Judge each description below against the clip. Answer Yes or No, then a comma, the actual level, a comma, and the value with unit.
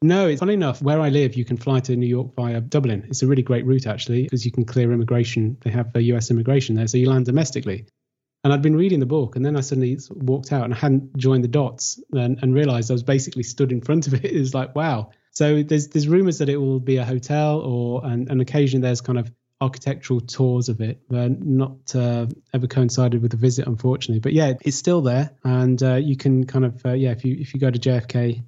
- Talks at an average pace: No, fast, 250 wpm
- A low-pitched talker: Yes, low, 130 Hz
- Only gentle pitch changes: Yes, narrow, 2.2 semitones